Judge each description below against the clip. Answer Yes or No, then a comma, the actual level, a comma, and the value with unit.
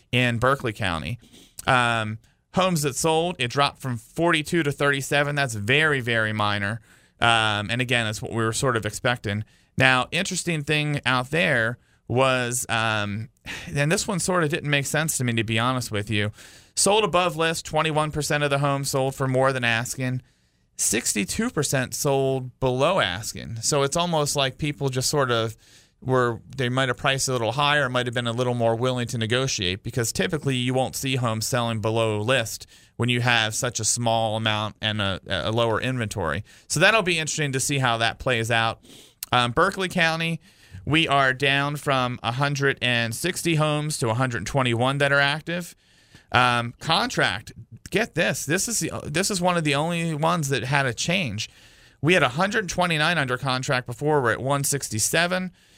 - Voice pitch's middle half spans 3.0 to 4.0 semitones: No, average, 4.6 semitones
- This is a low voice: Yes, low, 130 Hz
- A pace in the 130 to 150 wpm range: No, average, 175 wpm